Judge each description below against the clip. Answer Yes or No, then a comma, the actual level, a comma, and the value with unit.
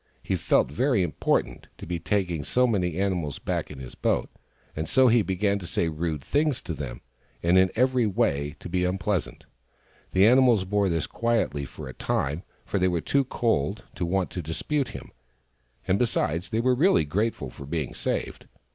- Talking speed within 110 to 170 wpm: No, average, 190 wpm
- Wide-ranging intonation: Yes, wide, 6.3 semitones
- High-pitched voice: No, very low, 95 Hz